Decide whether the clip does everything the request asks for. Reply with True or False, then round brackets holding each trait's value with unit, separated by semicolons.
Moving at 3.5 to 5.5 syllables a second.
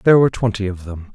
False (7.2 syllables/s)